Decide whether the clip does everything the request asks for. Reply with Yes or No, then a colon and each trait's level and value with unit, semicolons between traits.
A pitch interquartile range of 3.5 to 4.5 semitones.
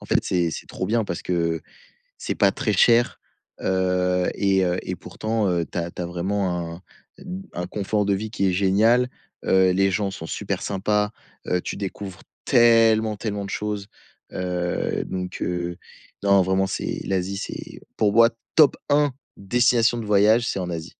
No: average, 3.1 semitones